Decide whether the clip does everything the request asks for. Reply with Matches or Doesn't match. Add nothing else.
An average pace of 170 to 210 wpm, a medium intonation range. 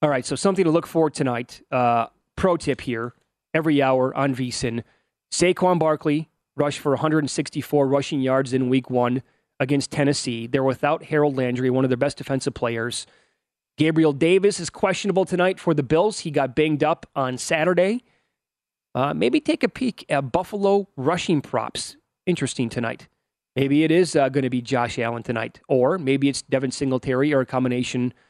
Matches